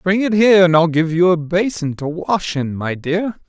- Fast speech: Yes, fast, 240 wpm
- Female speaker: No, male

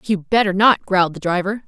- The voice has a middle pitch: No, high, 195 Hz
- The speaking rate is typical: No, fast, 215 wpm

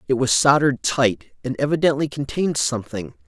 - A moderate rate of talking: Yes, average, 145 wpm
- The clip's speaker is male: Yes, male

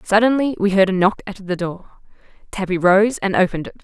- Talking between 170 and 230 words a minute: Yes, fast, 205 wpm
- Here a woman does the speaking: Yes, female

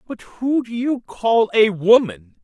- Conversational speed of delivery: Yes, average, 175 wpm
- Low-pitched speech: No, high, 215 Hz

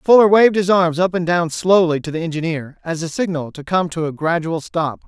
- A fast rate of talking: Yes, fast, 235 wpm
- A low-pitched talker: No, medium, 170 Hz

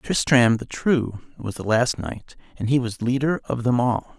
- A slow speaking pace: No, average, 200 wpm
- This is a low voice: Yes, low, 125 Hz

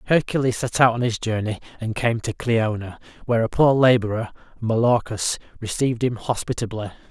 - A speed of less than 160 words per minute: Yes, average, 150 wpm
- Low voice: Yes, low, 115 Hz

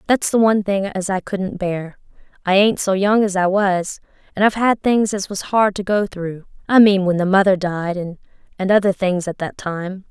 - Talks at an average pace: No, fast, 215 wpm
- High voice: Yes, high, 195 Hz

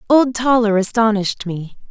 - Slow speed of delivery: Yes, slow, 125 wpm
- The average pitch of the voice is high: Yes, high, 220 Hz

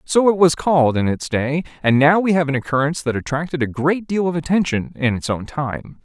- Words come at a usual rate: No, fast, 240 wpm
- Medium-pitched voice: Yes, medium, 150 Hz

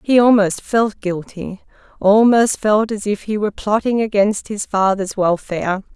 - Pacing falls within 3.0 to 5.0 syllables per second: Yes, 4.5 syllables/s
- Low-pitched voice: No, high, 205 Hz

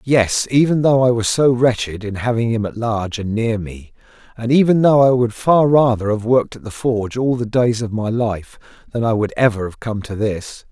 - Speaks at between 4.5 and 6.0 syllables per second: Yes, 5.1 syllables/s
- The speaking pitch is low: Yes, low, 115 Hz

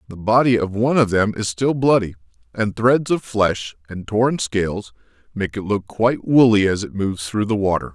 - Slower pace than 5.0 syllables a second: No, 5.2 syllables/s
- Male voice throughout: Yes, male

